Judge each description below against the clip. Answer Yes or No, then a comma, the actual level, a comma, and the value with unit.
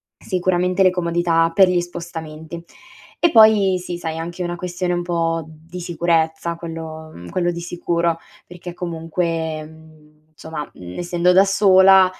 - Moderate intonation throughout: No, narrow, 1.9 semitones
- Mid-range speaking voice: Yes, medium, 170 Hz